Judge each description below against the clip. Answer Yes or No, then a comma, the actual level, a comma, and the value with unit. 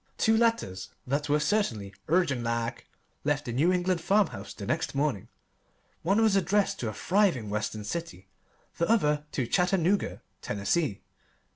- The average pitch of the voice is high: No, medium, 150 Hz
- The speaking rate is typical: Yes, average, 145 wpm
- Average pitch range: No, wide, 8.3 semitones